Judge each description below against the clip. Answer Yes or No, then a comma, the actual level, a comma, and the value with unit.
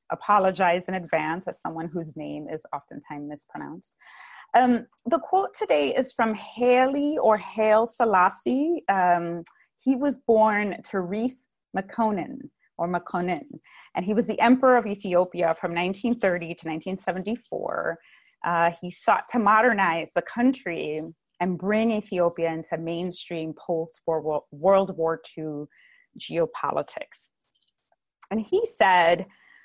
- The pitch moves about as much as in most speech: No, wide, 5.8 semitones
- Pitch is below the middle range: No, high, 190 Hz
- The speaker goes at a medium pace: No, slow, 120 wpm